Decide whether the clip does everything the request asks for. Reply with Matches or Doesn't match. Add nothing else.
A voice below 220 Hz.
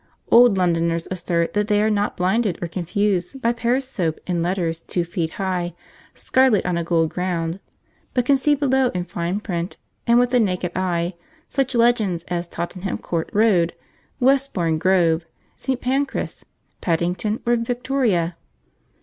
Matches